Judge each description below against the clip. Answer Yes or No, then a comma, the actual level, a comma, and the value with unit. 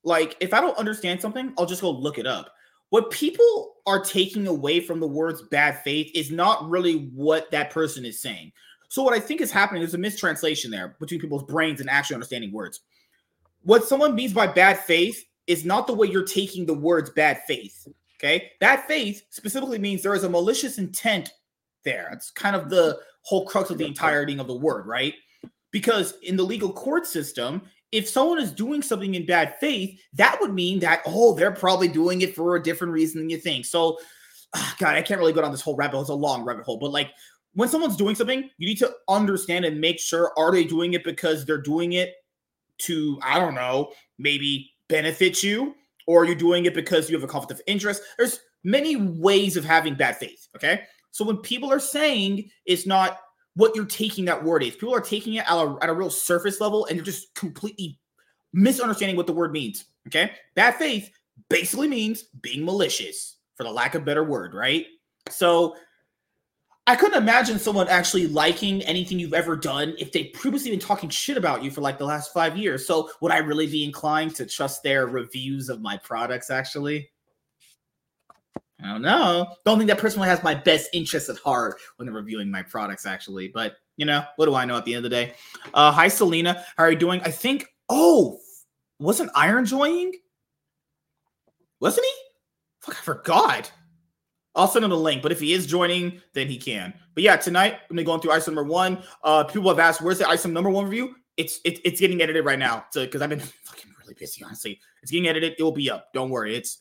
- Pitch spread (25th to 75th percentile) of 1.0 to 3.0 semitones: No, average, 5.1 semitones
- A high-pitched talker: No, medium, 175 Hz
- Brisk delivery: Yes, fast, 215 wpm